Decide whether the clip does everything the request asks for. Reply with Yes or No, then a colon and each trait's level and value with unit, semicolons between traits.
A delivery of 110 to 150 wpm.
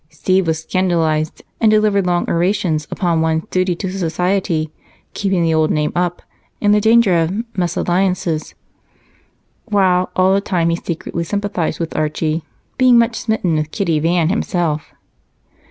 Yes: average, 145 wpm